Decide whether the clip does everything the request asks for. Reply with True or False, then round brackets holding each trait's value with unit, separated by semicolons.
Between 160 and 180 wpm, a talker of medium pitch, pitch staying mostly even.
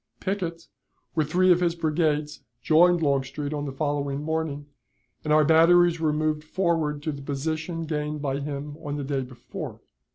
True (165 wpm; 150 Hz; 2.3 semitones)